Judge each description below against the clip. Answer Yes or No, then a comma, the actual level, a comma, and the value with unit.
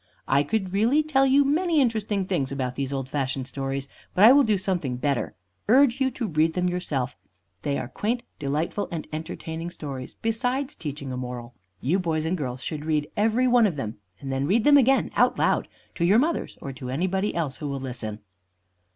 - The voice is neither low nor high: Yes, medium, 165 Hz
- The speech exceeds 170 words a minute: Yes, average, 200 wpm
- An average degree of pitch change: No, wide, 8.7 semitones